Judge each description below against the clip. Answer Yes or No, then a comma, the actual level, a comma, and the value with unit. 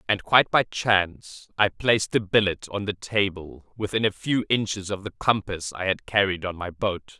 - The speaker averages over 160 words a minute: Yes, average, 200 wpm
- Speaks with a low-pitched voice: Yes, low, 100 Hz